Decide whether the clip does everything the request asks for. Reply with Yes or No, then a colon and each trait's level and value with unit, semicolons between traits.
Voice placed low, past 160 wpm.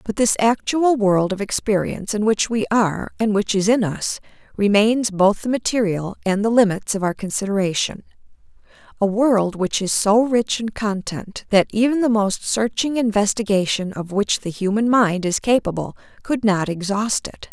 No: high, 210 Hz; average, 170 wpm